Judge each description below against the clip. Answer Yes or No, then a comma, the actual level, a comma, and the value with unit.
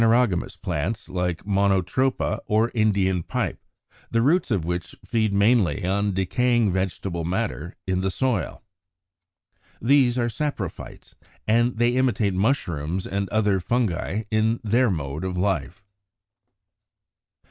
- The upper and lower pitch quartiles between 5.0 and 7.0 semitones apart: No, average, 4.3 semitones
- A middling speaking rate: No, slow, 125 wpm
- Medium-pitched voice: No, low, 100 Hz